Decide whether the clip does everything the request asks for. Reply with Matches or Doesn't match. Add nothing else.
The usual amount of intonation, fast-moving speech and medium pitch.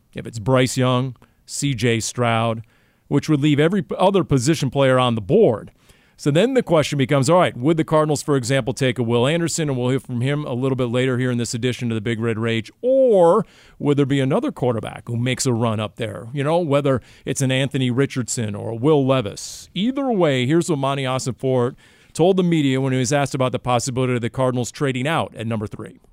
Doesn't match